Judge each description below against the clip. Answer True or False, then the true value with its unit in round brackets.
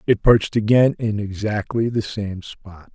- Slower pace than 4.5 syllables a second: True (4.3 syllables/s)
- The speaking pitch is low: True (105 Hz)